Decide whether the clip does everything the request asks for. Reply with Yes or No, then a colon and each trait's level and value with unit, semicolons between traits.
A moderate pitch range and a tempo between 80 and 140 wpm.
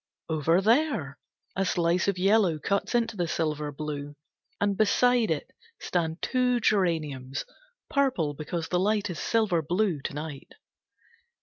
No: wide, 5.8 semitones; slow, 135 wpm